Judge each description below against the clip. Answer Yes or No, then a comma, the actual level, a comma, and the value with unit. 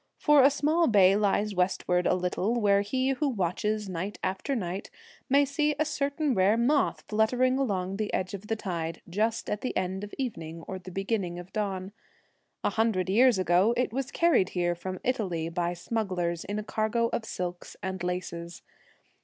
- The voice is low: No, high, 200 Hz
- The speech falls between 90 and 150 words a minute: No, average, 180 wpm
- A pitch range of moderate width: Yes, average, 4.8 semitones